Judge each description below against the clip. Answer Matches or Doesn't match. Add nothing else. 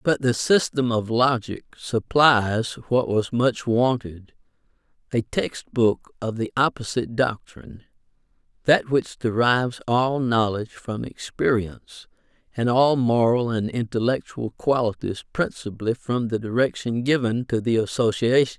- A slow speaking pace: Matches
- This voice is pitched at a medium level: Doesn't match